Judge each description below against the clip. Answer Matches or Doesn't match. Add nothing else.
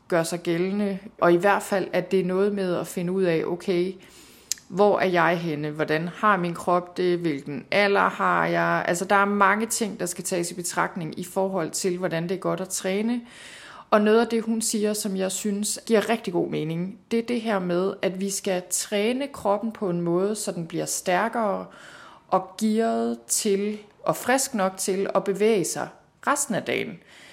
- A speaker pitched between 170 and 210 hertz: Matches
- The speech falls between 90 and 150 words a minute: Doesn't match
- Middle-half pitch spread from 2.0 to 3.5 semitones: Matches